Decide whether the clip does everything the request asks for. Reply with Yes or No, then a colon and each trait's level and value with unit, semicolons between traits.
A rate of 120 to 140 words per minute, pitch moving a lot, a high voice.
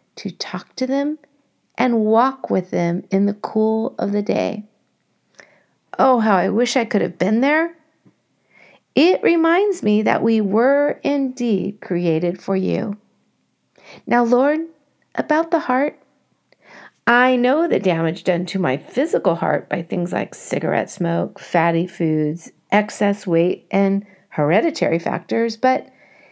Yes: slow, 135 wpm; wide, 5.9 semitones; high, 215 Hz